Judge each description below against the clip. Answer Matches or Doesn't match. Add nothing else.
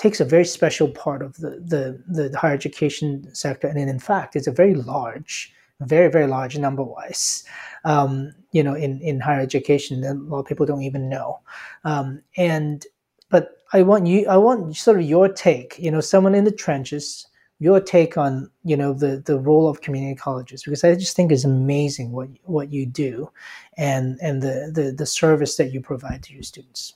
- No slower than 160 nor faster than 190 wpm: Doesn't match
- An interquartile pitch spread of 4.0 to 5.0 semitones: Doesn't match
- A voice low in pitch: Doesn't match